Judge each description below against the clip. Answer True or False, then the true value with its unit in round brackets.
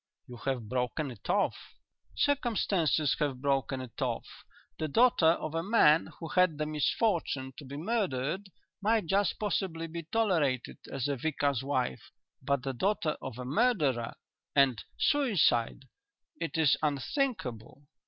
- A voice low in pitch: False (150 Hz)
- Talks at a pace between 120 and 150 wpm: True (140 wpm)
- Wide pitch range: True (6.3 semitones)